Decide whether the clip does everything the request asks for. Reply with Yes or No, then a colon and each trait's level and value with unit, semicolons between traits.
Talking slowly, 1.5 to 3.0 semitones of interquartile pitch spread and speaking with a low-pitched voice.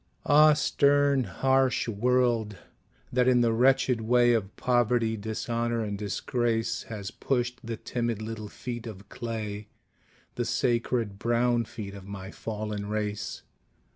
Yes: slow, 130 wpm; narrow, 2.6 semitones; low, 115 Hz